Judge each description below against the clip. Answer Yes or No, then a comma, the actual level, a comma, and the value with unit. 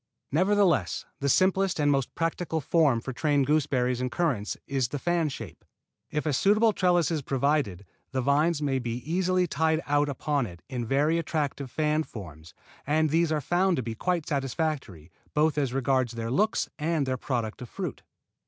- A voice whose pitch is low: No, medium, 145 Hz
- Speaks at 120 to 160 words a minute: No, average, 175 wpm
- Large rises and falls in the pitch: No, average, 4.3 semitones